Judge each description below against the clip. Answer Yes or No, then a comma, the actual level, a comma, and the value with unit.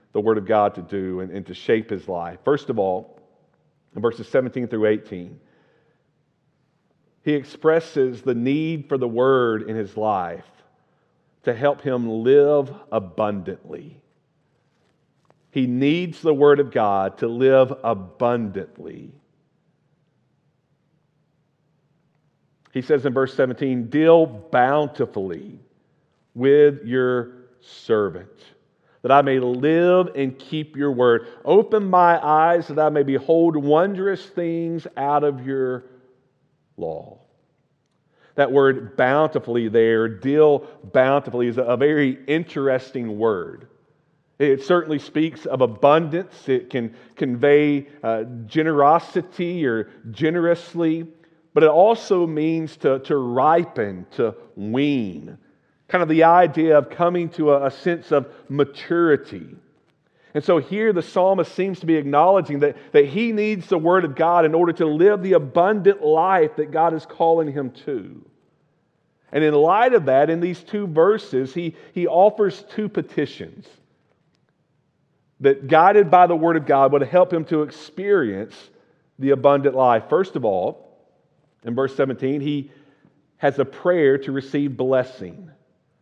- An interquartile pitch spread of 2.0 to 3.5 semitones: No, average, 4.0 semitones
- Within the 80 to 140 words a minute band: Yes, slow, 135 wpm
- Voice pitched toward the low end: No, medium, 145 Hz